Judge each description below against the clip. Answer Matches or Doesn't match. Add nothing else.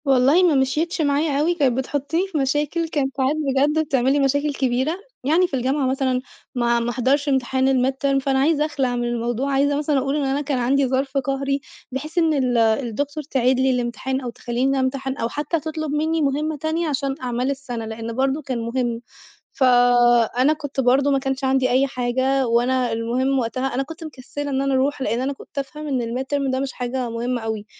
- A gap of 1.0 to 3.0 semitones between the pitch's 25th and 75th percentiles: Matches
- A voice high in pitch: Matches